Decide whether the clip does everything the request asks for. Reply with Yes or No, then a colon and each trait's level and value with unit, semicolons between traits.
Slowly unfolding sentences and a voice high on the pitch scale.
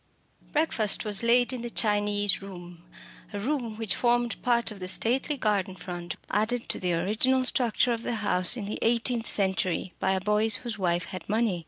No: average, 185 wpm; high, 215 Hz